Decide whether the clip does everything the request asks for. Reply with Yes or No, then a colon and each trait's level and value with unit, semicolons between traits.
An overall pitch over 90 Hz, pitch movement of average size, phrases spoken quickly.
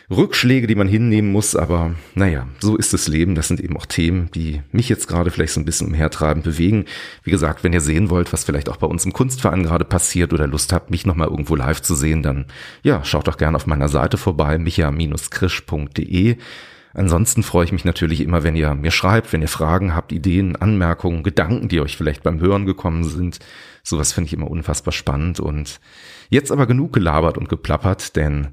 No: very low, 85 Hz; average, 3.4 semitones; fast, 205 wpm